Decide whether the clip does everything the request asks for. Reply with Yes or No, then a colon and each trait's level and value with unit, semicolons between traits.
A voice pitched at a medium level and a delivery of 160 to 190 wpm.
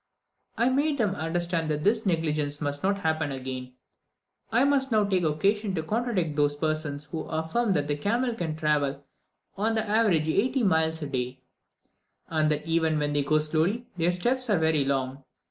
Yes: medium, 160 Hz; average, 175 wpm